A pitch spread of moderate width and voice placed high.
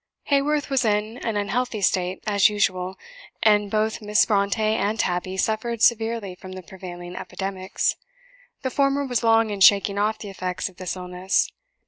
Yes: average, 3.1 semitones; high, 205 Hz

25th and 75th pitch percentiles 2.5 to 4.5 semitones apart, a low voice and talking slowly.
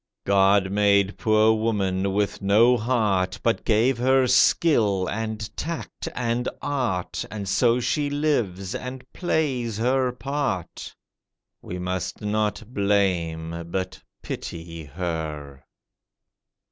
No: average, 4.9 semitones; low, 105 Hz; slow, 110 wpm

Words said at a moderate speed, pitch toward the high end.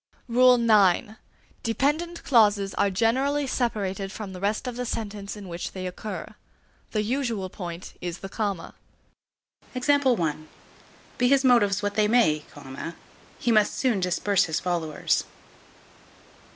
No: slow, 125 wpm; high, 210 Hz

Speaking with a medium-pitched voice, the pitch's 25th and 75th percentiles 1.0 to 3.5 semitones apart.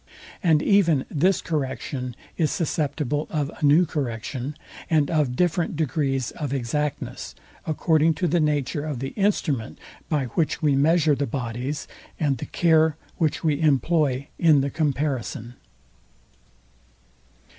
Yes: medium, 150 Hz; average, 2.9 semitones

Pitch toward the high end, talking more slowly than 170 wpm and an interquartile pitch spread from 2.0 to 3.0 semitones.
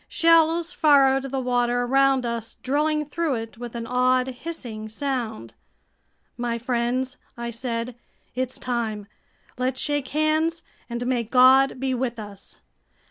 Yes: very high, 255 Hz; slow, 135 wpm; narrow, 2.4 semitones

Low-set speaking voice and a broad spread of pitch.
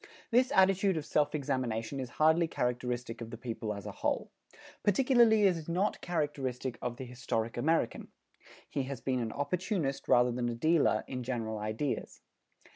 Yes: low, 130 Hz; wide, 5.7 semitones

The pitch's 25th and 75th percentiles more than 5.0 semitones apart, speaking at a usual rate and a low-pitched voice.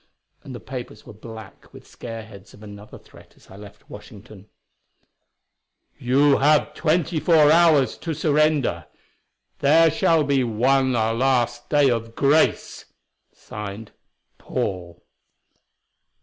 No: wide, 5.4 semitones; slow, 115 wpm; low, 125 Hz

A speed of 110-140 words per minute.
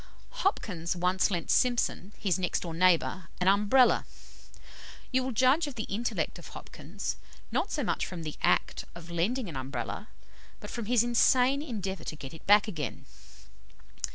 No: average, 160 wpm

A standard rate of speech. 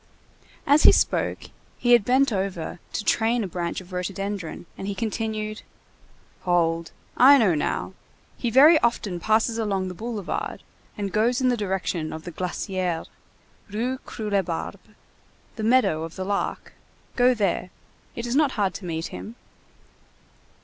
Yes: average, 150 wpm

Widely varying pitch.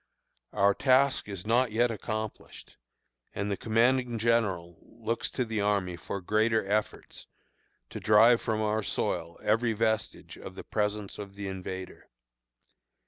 No: narrow, 2.5 semitones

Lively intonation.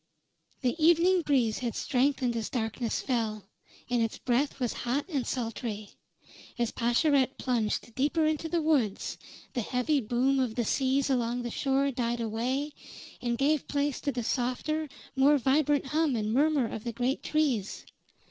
No: average, 3.4 semitones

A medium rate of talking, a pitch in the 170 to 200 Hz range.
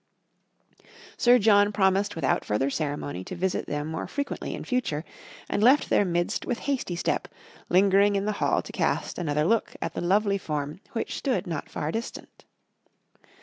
Yes: average, 165 wpm; high, 190 Hz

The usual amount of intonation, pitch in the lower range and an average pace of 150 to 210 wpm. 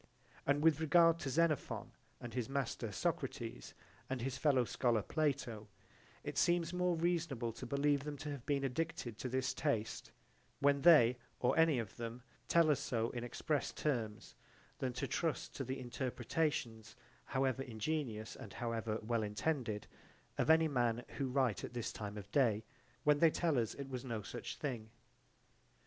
Yes: average, 4.4 semitones; low, 130 Hz; average, 165 wpm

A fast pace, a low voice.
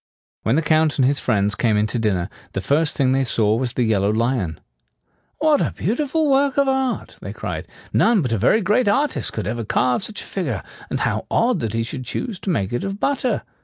Yes: fast, 225 wpm; low, 130 Hz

